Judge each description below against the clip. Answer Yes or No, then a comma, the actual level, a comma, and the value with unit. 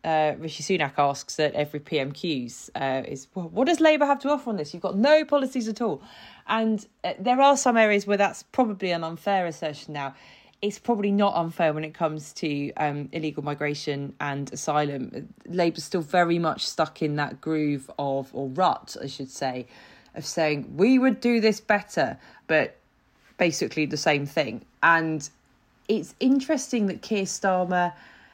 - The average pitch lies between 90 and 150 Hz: No, medium, 165 Hz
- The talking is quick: No, average, 175 wpm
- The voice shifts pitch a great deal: Yes, wide, 5.9 semitones